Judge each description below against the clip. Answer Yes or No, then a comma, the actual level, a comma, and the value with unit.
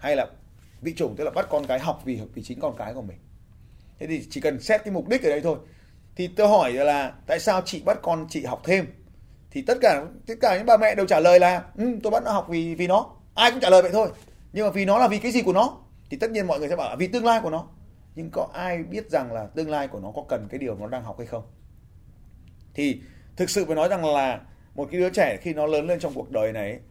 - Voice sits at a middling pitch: Yes, medium, 165 Hz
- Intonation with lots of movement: Yes, wide, 8.0 semitones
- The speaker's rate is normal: No, fast, 285 wpm